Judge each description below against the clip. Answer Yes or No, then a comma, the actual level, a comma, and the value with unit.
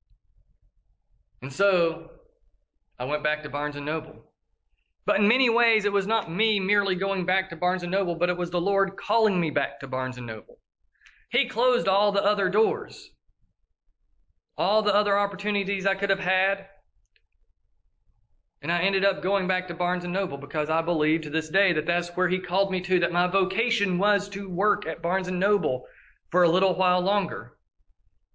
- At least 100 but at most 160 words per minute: No, average, 185 wpm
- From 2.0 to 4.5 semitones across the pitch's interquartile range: No, average, 5.0 semitones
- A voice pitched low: No, medium, 185 Hz